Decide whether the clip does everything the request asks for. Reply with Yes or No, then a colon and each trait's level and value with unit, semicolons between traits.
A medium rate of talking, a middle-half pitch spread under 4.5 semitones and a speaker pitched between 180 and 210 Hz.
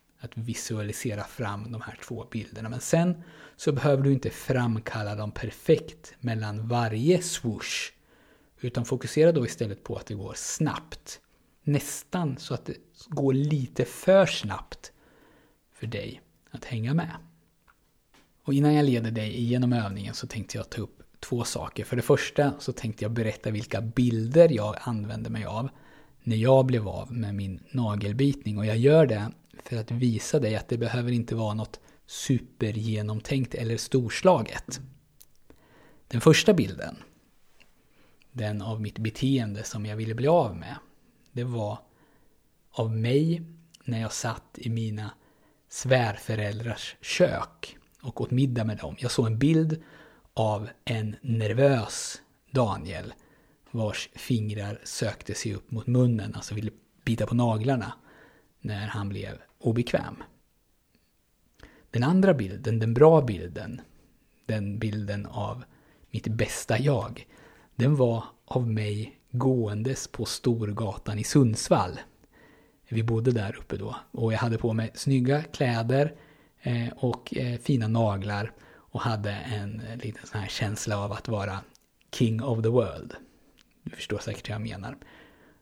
No: average, 140 wpm; average, 3.7 semitones; low, 115 Hz